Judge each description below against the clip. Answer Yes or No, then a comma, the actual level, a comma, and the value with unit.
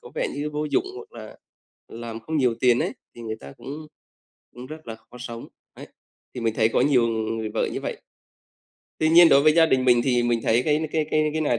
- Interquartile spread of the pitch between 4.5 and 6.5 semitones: Yes, average, 4.8 semitones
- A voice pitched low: Yes, low, 125 Hz